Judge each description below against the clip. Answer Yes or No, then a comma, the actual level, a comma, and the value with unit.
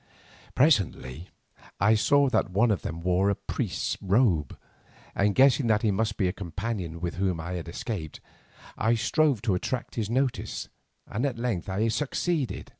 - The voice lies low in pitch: Yes, low, 105 Hz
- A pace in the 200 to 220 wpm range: No, average, 160 wpm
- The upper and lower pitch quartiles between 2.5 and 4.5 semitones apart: No, average, 5.1 semitones